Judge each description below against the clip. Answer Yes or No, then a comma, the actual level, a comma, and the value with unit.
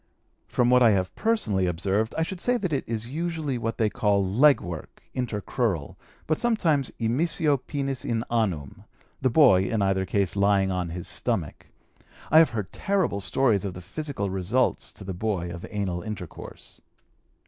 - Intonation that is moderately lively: No, wide, 6.3 semitones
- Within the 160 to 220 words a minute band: Yes, average, 170 wpm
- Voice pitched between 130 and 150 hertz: No, low, 110 Hz